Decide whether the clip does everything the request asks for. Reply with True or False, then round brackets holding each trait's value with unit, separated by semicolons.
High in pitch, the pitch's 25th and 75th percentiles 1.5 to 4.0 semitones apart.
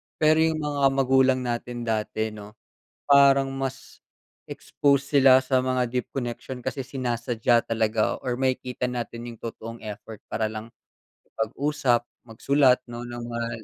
False (125 Hz; 2.5 semitones)